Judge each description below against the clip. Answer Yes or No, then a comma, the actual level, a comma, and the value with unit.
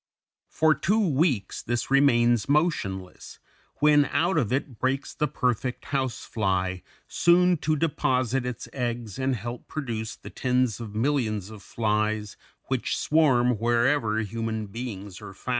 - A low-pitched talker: Yes, low, 125 Hz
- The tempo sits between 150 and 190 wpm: No, average, 140 wpm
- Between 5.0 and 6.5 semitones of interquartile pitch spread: No, average, 4.6 semitones